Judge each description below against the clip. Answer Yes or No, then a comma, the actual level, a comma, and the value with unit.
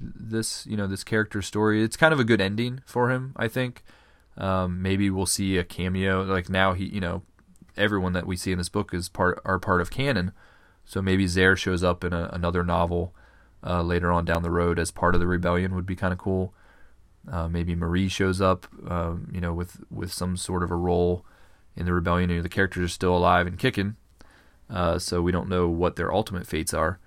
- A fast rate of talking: Yes, fast, 225 wpm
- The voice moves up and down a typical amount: No, narrow, 1.8 semitones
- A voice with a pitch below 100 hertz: Yes, very low, 90 Hz